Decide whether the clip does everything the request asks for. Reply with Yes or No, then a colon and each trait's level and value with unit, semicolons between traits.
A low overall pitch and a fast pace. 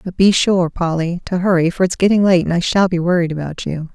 No: medium, 175 Hz; fast, 260 wpm